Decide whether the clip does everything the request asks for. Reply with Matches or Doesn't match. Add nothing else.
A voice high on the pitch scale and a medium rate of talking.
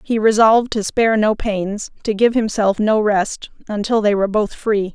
Matches